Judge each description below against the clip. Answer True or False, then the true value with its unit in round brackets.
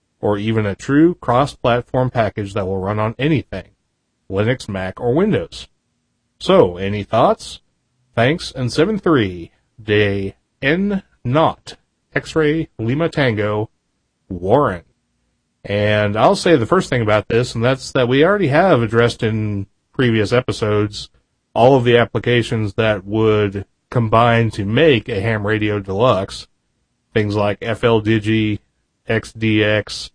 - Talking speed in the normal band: False (125 wpm)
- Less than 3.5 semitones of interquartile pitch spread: True (3.1 semitones)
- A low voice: True (110 Hz)